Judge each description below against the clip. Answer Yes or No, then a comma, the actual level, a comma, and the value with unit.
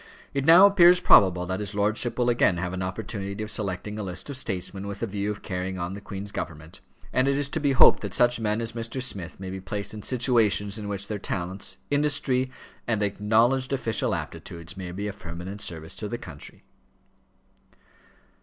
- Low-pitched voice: Yes, low, 105 Hz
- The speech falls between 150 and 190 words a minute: No, average, 200 wpm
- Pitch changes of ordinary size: Yes, average, 4.2 semitones